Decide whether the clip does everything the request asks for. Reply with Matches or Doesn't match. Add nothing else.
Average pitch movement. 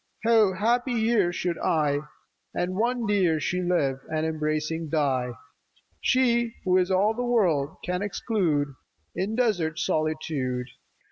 Doesn't match